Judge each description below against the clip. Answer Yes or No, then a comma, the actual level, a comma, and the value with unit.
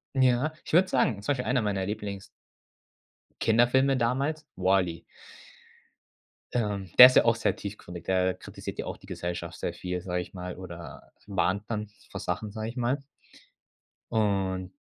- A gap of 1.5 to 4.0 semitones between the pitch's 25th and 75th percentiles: No, average, 4.8 semitones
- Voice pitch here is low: Yes, low, 105 Hz